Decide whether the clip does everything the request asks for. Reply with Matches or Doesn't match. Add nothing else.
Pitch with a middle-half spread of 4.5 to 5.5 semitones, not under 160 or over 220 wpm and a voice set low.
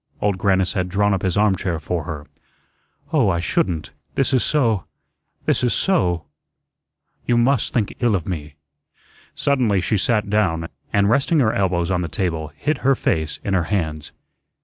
Matches